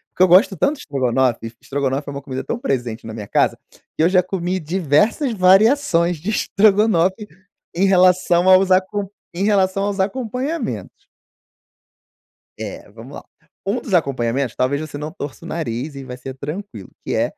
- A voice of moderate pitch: Yes, medium, 180 Hz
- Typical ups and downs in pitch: No, wide, 6.2 semitones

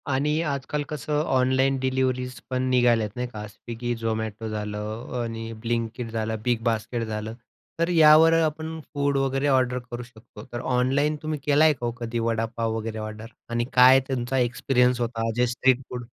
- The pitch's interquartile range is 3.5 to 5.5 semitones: No, average, 2.8 semitones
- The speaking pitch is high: No, low, 125 Hz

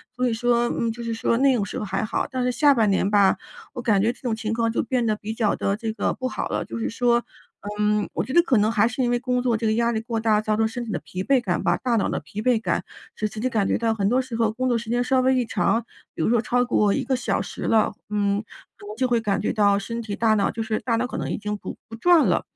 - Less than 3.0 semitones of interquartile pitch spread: Yes, narrow, 2.5 semitones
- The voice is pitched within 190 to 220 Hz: No, high, 230 Hz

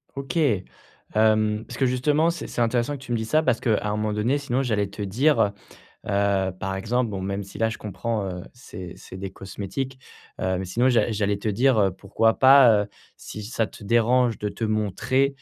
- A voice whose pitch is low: Yes, low, 110 Hz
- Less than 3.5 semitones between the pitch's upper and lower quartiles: No, average, 3.8 semitones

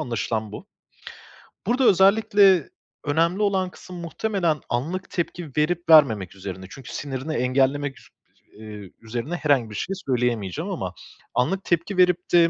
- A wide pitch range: Yes, wide, 7.0 semitones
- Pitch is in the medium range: Yes, medium, 150 Hz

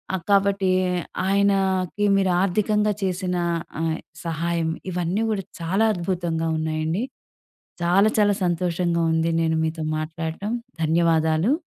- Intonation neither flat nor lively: Yes, average, 3.3 semitones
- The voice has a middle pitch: Yes, medium, 175 Hz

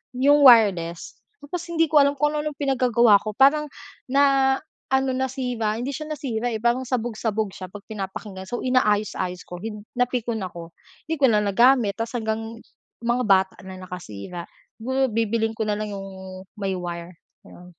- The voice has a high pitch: Yes, high, 225 Hz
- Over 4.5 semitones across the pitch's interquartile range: Yes, average, 5.0 semitones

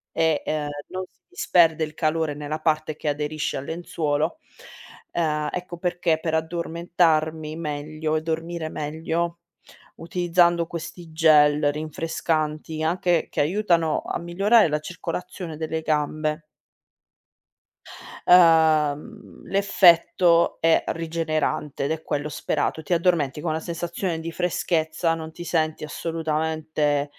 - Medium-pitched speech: Yes, medium, 160 Hz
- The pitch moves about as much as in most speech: No, narrow, 1.8 semitones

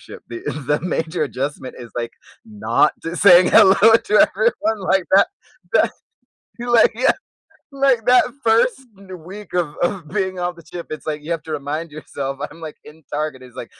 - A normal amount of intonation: No, wide, 5.7 semitones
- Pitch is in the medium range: Yes, medium, 175 Hz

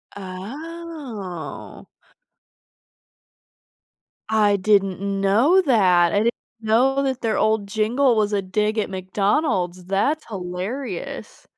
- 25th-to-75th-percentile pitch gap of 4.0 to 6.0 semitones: Yes, average, 4.7 semitones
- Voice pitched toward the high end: Yes, high, 210 Hz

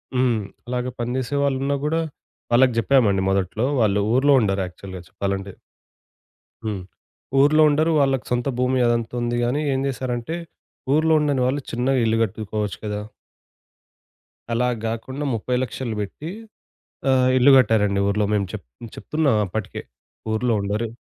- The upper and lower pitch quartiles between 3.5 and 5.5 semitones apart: Yes, average, 4.1 semitones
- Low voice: Yes, low, 120 Hz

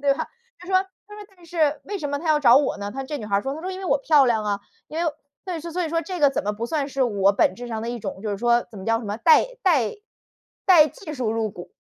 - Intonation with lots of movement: Yes, wide, 6.7 semitones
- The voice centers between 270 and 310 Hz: Yes, very high, 275 Hz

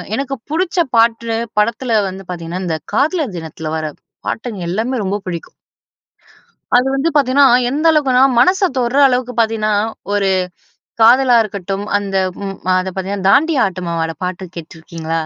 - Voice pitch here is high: Yes, high, 215 Hz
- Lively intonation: Yes, wide, 5.8 semitones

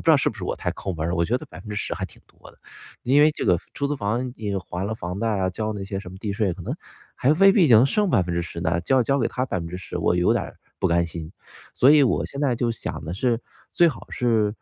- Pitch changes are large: Yes, wide, 6.3 semitones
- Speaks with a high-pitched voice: No, low, 105 Hz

